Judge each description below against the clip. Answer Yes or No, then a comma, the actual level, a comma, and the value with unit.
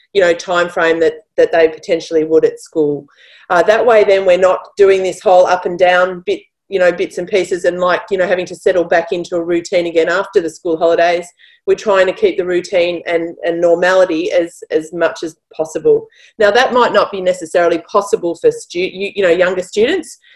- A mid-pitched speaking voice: Yes, medium, 180 Hz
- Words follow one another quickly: Yes, fast, 215 wpm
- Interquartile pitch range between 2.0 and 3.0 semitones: No, average, 4.2 semitones